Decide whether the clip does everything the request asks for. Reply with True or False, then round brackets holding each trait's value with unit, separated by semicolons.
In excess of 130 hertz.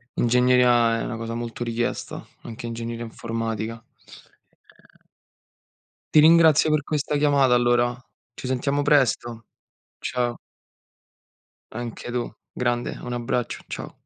False (120 Hz)